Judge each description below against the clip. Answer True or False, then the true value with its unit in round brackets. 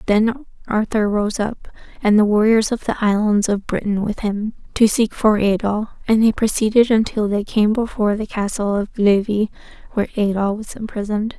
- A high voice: True (210 Hz)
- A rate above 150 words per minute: True (175 wpm)